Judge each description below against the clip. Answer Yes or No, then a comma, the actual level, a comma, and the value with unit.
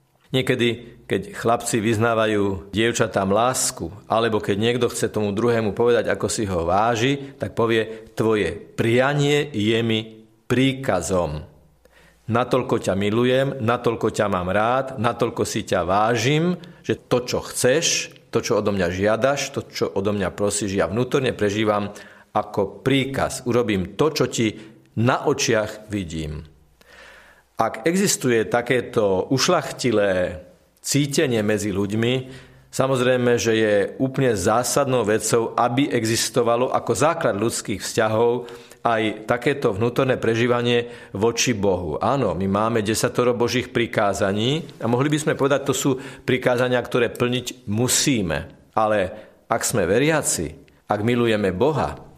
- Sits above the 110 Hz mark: Yes, low, 120 Hz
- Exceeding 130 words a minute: No, average, 125 wpm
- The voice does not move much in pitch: No, average, 3.1 semitones